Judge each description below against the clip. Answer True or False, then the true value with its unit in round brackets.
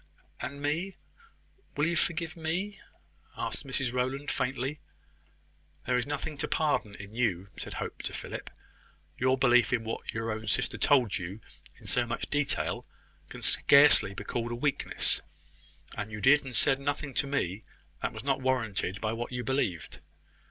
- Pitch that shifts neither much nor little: True (4.2 semitones)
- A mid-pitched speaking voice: False (130 Hz)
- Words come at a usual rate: True (165 wpm)